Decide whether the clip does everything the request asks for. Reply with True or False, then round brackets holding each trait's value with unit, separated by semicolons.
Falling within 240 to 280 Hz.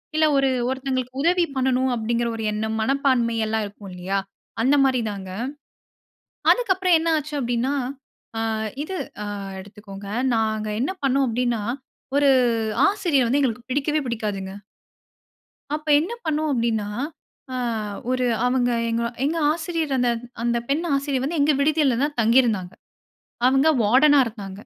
True (255 Hz)